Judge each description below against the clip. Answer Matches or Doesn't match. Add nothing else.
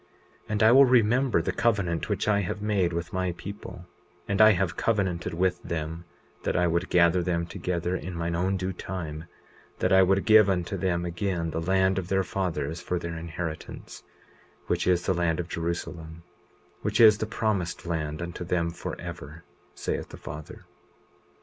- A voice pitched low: Matches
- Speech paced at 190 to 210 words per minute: Doesn't match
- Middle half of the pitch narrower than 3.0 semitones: Matches